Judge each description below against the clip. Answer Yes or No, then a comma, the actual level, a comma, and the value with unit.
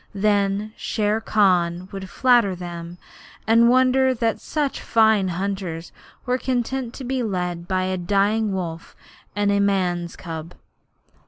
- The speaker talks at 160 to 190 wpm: No, average, 140 wpm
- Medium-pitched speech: No, high, 200 Hz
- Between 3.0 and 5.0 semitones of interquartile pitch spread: Yes, average, 4.2 semitones